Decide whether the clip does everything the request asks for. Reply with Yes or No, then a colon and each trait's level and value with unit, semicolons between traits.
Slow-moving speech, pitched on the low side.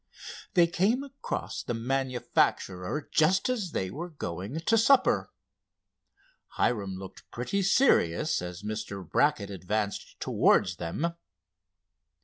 Yes: slow, 110 wpm; low, 125 Hz